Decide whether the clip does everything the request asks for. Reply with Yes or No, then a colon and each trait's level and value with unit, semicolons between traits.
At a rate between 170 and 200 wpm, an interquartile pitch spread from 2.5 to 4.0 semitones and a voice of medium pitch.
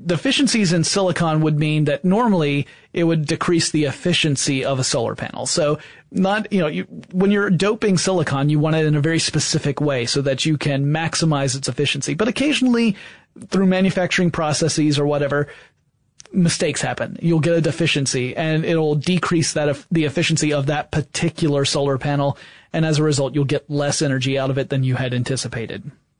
Yes: average, 180 wpm; average, 3.6 semitones; medium, 155 Hz